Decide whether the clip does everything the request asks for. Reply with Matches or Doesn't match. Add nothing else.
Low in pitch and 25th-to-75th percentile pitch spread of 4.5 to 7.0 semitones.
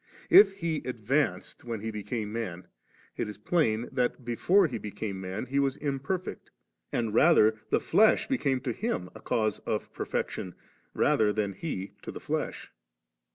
Matches